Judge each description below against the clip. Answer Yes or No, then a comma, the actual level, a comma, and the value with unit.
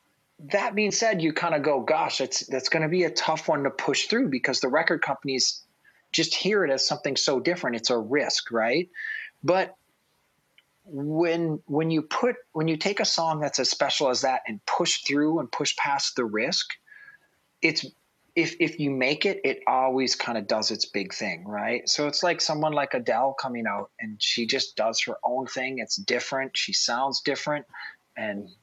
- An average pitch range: No, wide, 5.7 semitones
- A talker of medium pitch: Yes, medium, 160 Hz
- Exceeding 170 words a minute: Yes, average, 195 wpm